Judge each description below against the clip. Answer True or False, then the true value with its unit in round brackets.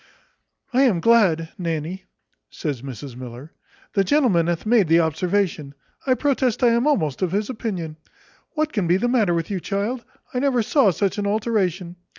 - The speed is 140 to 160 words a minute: False (170 wpm)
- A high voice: True (195 Hz)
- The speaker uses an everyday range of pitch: False (6.1 semitones)